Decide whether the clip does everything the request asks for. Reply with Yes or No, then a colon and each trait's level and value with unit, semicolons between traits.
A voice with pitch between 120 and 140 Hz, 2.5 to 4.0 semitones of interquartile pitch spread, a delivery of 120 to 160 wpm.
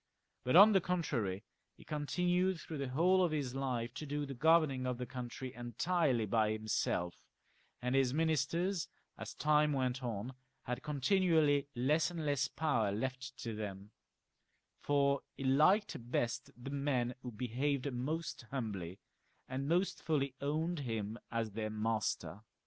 No: low, 135 Hz; average, 4.4 semitones; average, 150 wpm